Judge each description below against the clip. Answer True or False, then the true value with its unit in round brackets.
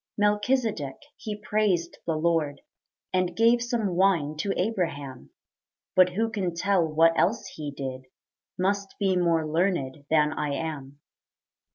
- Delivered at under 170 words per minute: True (135 wpm)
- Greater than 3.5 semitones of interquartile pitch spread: True (4.9 semitones)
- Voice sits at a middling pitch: True (175 Hz)